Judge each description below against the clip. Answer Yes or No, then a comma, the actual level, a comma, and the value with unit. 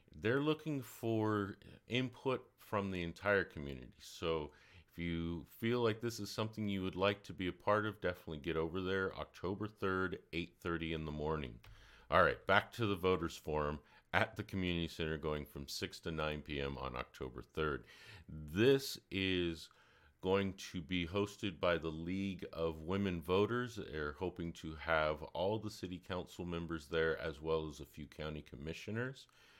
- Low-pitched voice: Yes, very low, 90 Hz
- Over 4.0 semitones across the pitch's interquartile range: Yes, average, 4.4 semitones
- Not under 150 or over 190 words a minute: Yes, average, 170 wpm